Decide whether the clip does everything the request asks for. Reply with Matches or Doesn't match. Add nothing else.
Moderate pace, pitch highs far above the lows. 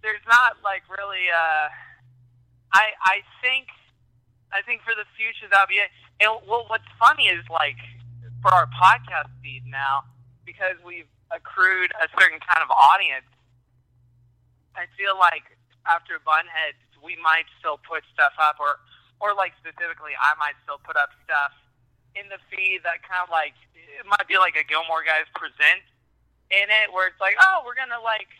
Matches